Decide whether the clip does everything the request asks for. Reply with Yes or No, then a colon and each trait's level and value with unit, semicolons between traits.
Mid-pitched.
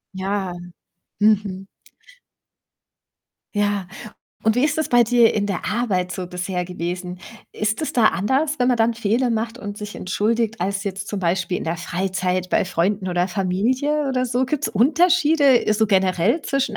No: high, 210 Hz